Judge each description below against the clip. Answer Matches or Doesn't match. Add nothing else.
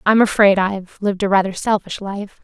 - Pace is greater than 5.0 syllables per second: Matches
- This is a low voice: Doesn't match